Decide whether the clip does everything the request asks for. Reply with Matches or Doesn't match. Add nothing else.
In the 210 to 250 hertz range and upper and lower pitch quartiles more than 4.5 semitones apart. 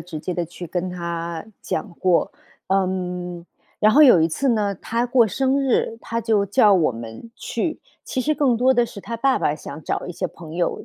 Doesn't match